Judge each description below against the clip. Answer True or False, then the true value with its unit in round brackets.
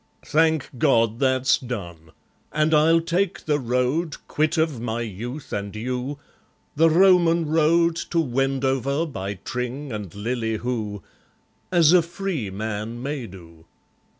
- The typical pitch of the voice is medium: False (130 Hz)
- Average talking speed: False (130 wpm)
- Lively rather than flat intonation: True (6.0 semitones)